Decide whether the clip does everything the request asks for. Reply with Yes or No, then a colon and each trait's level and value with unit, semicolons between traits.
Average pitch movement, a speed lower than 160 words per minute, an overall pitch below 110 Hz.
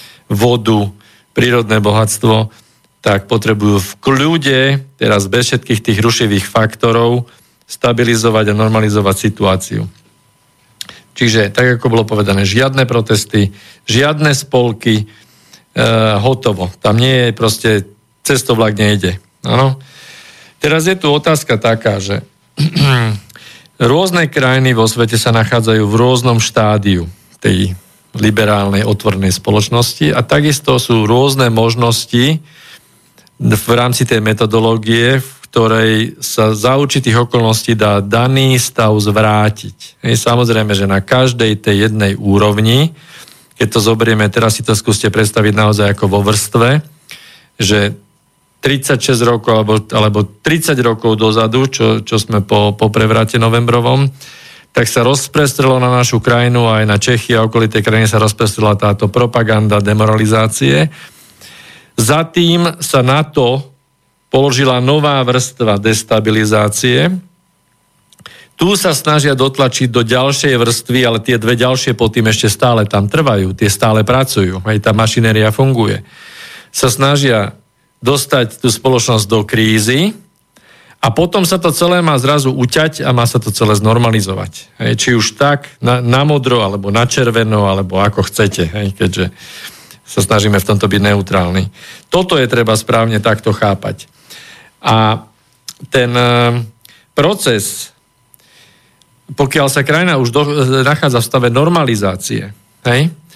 No: average, 3.4 semitones; average, 125 wpm; low, 115 Hz